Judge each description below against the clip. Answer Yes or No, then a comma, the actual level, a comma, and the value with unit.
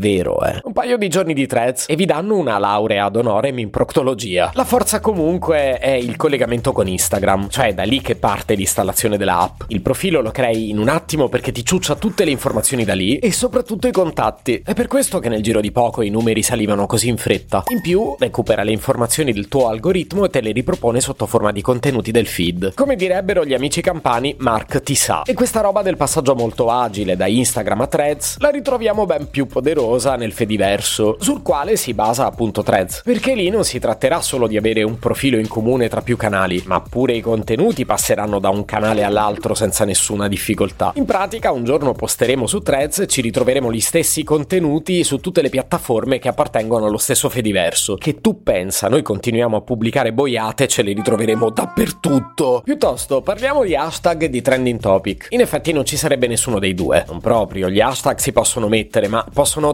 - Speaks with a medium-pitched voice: No, low, 125 Hz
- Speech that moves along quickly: Yes, fast, 200 wpm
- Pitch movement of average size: No, wide, 6.5 semitones